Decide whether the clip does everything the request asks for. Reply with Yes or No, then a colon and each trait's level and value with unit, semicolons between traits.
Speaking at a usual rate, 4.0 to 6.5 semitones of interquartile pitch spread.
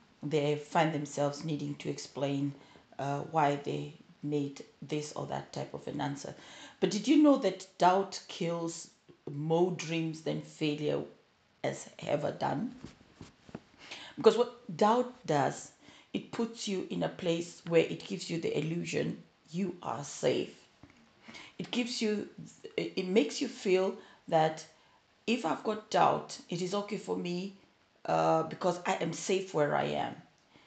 Yes: average, 145 wpm; average, 5.3 semitones